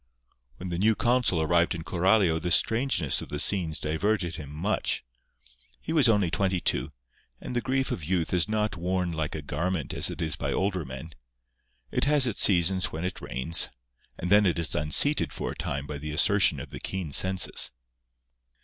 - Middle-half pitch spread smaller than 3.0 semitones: No, average, 4.3 semitones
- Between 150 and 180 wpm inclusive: No, average, 190 wpm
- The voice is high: No, very low, 90 Hz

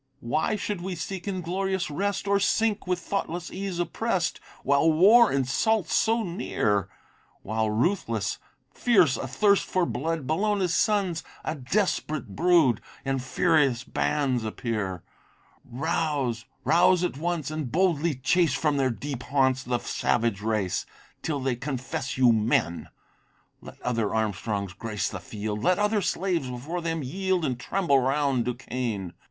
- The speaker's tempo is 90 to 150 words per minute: Yes, slow, 135 wpm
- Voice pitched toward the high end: No, medium, 150 Hz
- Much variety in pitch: Yes, wide, 6.8 semitones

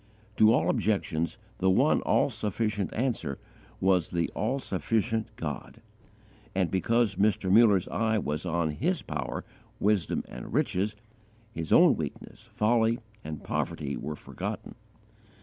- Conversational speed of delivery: No, slow, 130 wpm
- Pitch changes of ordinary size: Yes, average, 4.4 semitones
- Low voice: Yes, low, 100 Hz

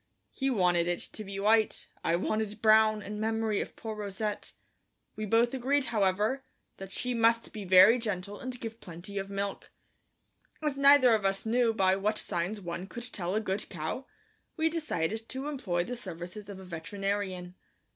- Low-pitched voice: No, high, 210 Hz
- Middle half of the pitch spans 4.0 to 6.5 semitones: No, average, 3.4 semitones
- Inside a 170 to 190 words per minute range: Yes, average, 175 wpm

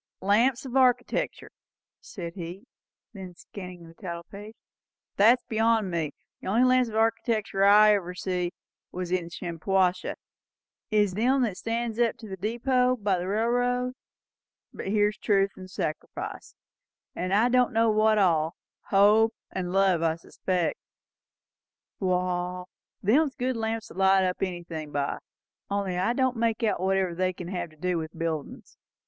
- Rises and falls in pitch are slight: No, average, 4.0 semitones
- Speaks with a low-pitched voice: No, high, 195 Hz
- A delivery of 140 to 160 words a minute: Yes, average, 155 wpm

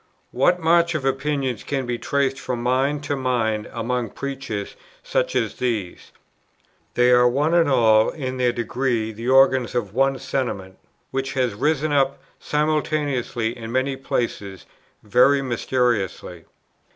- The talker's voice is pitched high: No, low, 130 Hz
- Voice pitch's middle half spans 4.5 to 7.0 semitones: No, average, 2.9 semitones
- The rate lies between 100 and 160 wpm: Yes, average, 140 wpm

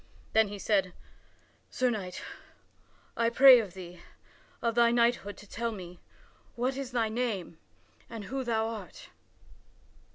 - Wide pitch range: No, average, 3.3 semitones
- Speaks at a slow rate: Yes, slow, 130 wpm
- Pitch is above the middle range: Yes, high, 225 Hz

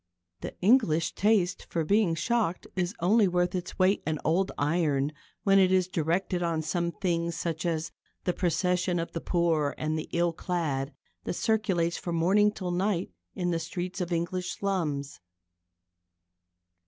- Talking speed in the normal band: Yes, average, 155 wpm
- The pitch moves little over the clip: Yes, narrow, 2.1 semitones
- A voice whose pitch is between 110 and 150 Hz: No, medium, 175 Hz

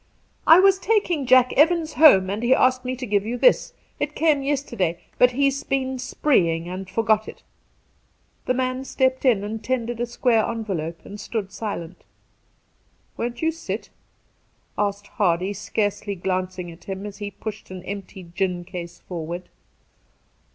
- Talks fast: No, average, 165 wpm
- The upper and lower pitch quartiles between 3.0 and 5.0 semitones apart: No, wide, 5.5 semitones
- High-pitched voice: Yes, high, 220 Hz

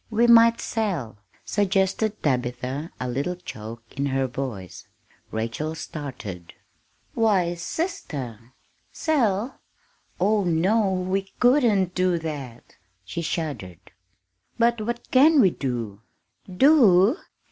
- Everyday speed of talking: No, slow, 105 wpm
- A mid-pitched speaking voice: Yes, medium, 175 Hz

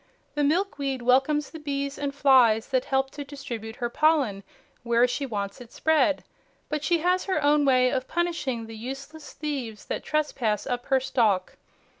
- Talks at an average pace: Yes, average, 170 wpm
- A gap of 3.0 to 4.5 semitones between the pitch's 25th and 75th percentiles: Yes, average, 3.6 semitones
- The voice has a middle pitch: No, very high, 270 Hz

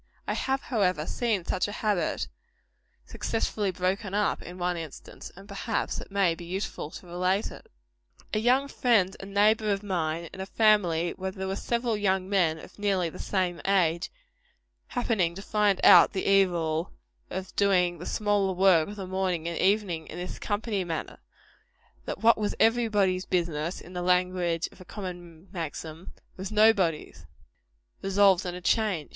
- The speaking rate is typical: Yes, average, 170 wpm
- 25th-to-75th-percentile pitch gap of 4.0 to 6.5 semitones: No, average, 2.8 semitones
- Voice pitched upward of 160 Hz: Yes, high, 190 Hz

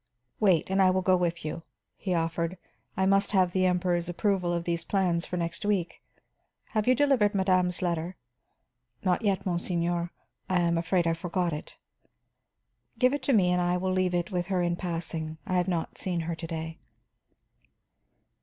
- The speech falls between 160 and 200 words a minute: Yes, average, 180 wpm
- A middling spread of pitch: No, narrow, 1.9 semitones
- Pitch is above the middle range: No, medium, 180 Hz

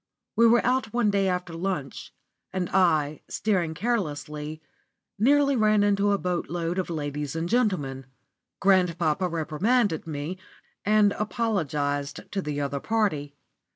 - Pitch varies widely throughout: Yes, wide, 5.8 semitones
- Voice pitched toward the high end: No, medium, 180 Hz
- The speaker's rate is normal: No, slow, 125 wpm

